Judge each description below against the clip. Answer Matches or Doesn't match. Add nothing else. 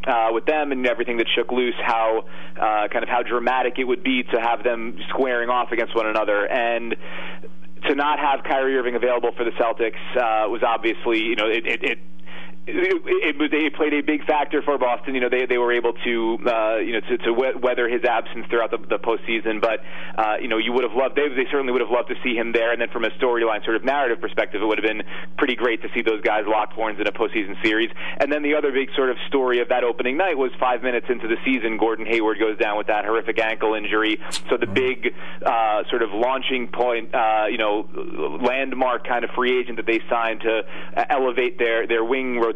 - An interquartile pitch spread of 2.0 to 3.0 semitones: Matches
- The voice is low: Matches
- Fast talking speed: Matches